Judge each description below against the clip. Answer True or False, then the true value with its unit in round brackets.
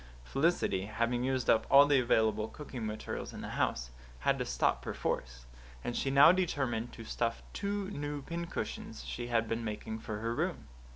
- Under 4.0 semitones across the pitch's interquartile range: False (4.5 semitones)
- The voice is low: True (120 Hz)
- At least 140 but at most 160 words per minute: False (175 wpm)